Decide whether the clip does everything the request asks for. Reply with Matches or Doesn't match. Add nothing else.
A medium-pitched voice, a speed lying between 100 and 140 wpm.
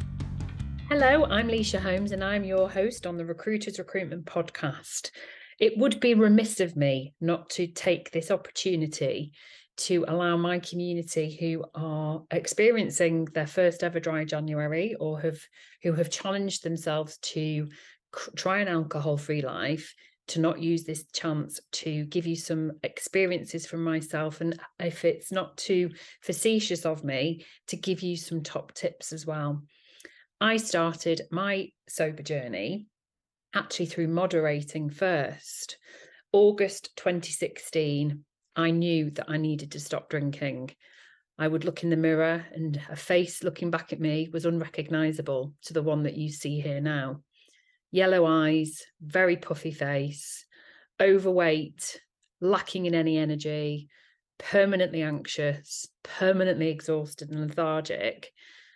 Matches